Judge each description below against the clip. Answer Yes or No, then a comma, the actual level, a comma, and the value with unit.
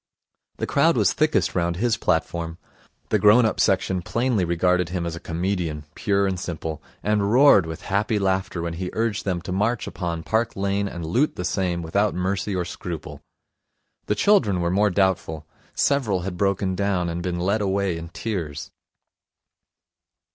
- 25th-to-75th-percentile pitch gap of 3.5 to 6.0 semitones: No, average, 2.9 semitones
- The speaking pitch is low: Yes, very low, 95 Hz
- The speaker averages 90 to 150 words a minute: No, average, 170 wpm